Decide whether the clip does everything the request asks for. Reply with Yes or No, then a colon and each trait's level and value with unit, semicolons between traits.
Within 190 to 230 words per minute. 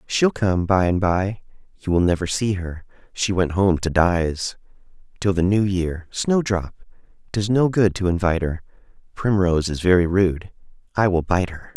No: average, 175 wpm